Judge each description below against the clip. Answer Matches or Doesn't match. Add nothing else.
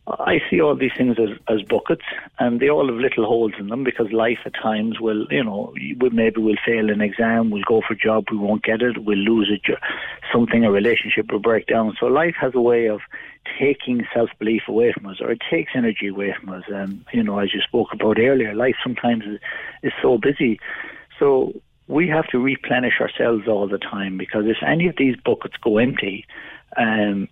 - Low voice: Matches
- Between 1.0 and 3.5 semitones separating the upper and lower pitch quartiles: Matches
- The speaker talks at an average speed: Doesn't match